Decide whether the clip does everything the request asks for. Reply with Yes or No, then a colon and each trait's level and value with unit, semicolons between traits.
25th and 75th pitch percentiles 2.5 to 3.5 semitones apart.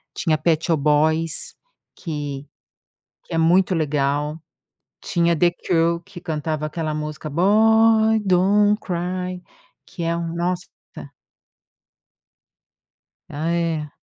Yes: average, 2.9 semitones